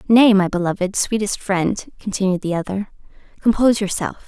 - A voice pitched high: Yes, high, 200 Hz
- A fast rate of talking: No, average, 140 wpm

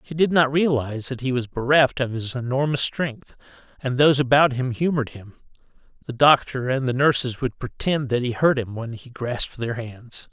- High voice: No, low, 130 Hz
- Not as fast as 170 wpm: No, average, 200 wpm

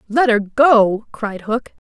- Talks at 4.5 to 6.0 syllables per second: No, 3.2 syllables/s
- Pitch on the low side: No, high, 230 Hz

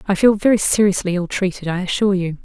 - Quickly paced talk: Yes, fast, 220 wpm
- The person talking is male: No, female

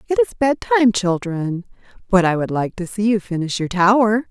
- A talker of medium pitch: No, high, 205 Hz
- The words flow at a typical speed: No, fast, 210 wpm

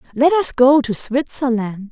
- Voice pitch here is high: Yes, very high, 255 Hz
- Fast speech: No, average, 155 wpm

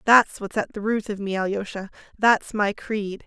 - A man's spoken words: No, female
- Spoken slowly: No, average, 200 wpm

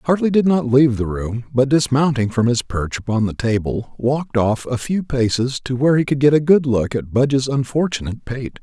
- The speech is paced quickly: Yes, fast, 215 wpm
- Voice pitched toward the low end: Yes, low, 130 Hz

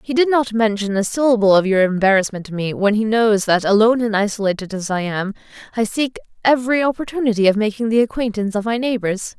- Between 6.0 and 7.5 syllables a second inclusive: Yes, 6.3 syllables/s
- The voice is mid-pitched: No, high, 220 Hz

